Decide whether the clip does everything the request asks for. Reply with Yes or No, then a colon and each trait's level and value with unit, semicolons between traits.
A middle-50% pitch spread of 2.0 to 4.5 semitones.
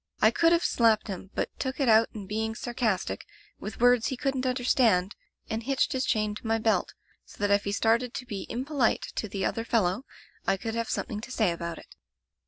Yes: average, 3.2 semitones